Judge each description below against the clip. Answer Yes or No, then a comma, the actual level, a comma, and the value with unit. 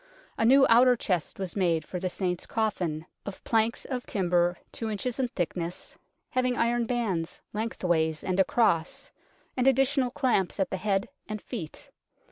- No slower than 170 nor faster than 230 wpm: No, average, 155 wpm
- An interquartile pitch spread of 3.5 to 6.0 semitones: Yes, average, 5.2 semitones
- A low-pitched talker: No, high, 205 Hz